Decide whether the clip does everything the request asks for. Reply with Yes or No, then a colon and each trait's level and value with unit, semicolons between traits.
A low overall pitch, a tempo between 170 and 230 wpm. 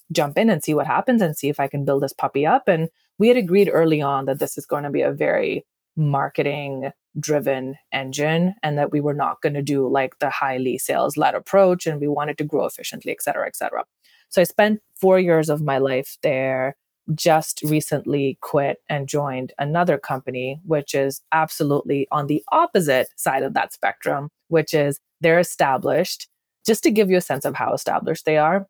No: medium, 150 Hz; fast, 205 wpm